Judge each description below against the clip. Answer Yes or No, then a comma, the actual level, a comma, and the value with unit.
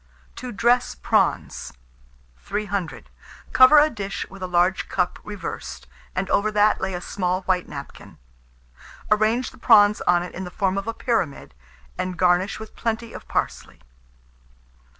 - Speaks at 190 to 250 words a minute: No, average, 150 wpm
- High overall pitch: Yes, high, 195 Hz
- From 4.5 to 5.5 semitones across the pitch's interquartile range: No, average, 3.2 semitones